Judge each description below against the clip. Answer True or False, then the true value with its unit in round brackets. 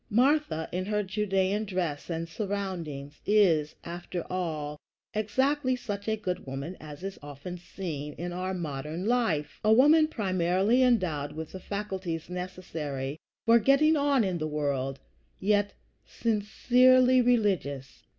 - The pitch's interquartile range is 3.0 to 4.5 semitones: False (5.5 semitones)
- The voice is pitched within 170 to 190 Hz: True (185 Hz)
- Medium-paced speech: False (130 wpm)